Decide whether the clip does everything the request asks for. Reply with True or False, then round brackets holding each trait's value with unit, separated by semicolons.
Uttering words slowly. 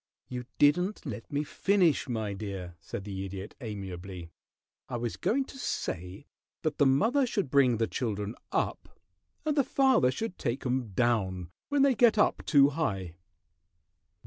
False (155 wpm)